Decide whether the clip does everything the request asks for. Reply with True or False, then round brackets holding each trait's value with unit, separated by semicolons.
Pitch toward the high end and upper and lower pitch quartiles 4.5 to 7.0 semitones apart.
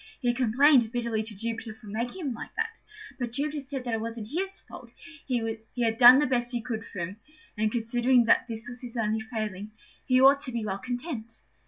False (235 Hz; 2.4 semitones)